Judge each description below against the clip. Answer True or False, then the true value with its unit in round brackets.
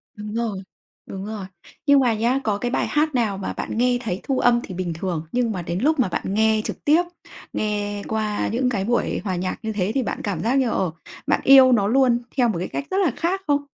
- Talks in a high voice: True (220 Hz)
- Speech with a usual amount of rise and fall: True (4.3 semitones)